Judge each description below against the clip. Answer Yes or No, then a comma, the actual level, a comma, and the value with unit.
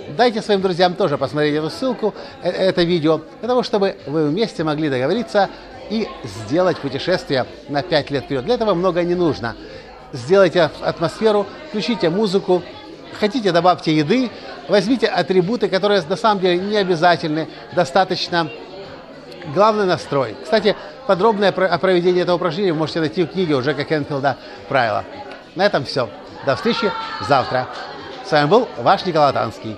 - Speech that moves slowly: No, average, 150 wpm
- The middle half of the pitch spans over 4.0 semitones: Yes, average, 4.6 semitones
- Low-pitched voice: No, medium, 180 Hz